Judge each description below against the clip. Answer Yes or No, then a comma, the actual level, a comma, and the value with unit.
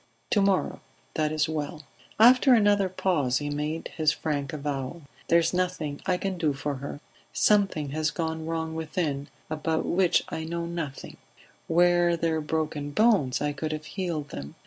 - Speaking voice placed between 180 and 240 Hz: No, medium, 160 Hz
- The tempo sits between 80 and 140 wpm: No, average, 165 wpm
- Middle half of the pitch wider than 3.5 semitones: No, average, 3.0 semitones